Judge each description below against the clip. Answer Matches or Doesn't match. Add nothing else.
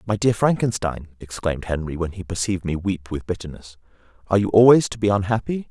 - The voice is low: Matches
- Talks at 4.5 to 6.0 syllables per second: Doesn't match